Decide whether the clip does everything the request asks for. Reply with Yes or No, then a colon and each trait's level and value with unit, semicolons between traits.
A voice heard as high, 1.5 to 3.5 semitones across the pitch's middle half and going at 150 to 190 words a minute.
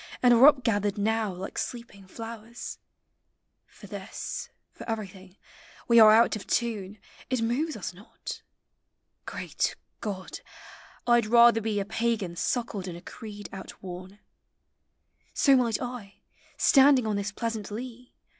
No: high, 220 Hz; average, 2.9 semitones; average, 140 wpm